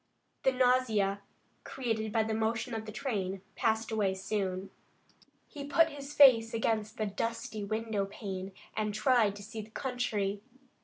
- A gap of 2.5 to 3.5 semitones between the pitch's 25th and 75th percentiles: Yes, average, 3.1 semitones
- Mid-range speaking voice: No, high, 220 Hz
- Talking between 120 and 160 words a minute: Yes, average, 150 wpm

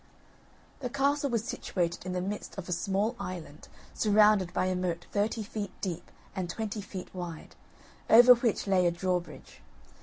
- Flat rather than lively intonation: No, average, 3.3 semitones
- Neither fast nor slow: Yes, average, 160 wpm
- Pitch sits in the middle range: No, high, 195 Hz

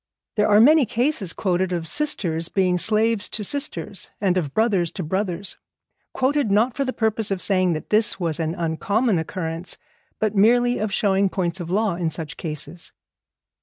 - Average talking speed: Yes, average, 170 wpm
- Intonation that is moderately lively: Yes, average, 4.4 semitones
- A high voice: Yes, high, 195 Hz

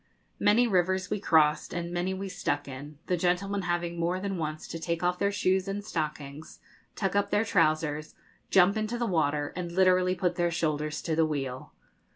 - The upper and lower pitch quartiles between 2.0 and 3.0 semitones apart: No, average, 3.4 semitones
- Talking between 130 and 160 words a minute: No, average, 190 wpm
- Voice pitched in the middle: Yes, medium, 175 Hz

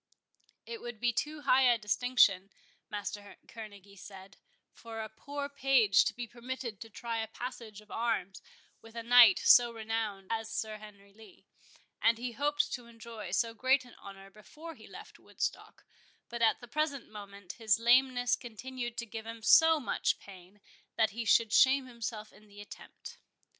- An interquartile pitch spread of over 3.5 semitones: No, average, 2.8 semitones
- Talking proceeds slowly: No, average, 170 wpm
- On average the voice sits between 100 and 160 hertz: No, high, 230 Hz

